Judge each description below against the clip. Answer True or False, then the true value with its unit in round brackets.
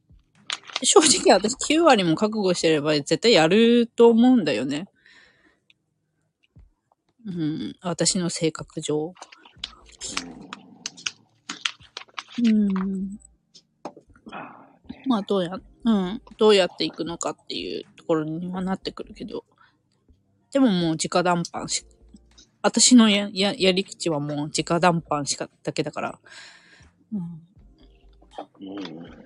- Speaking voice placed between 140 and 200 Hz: True (185 Hz)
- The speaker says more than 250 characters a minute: False (195 characters per minute)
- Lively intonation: True (5.8 semitones)